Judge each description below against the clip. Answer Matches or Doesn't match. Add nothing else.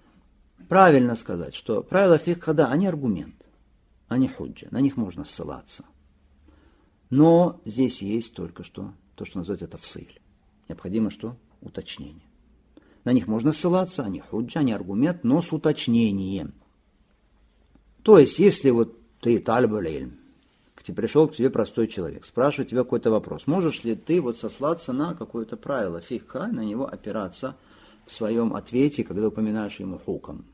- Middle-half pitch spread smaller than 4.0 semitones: Doesn't match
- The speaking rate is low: Doesn't match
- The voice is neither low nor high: Doesn't match